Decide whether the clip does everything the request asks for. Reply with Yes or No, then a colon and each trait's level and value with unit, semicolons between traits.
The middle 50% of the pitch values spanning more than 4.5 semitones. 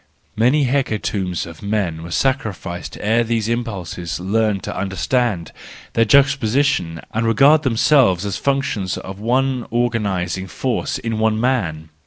Yes: average, 5.0 semitones